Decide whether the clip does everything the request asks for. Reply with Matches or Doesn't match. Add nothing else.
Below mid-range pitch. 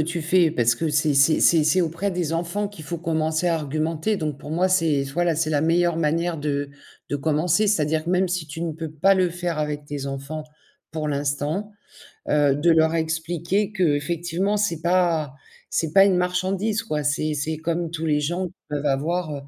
Doesn't match